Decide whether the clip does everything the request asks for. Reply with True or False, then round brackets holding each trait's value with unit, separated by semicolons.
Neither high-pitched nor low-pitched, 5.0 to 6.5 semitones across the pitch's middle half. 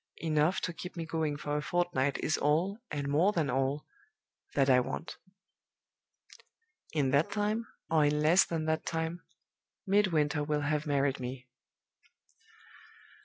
False (150 Hz; 2.7 semitones)